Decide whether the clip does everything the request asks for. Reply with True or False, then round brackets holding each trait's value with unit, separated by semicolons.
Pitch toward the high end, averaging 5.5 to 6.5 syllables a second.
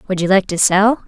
True (195 Hz; 5.7 syllables/s)